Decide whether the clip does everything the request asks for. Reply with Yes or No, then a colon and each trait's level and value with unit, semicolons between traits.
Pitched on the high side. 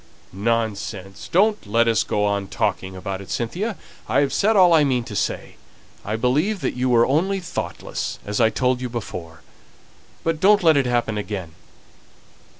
No: low, 120 Hz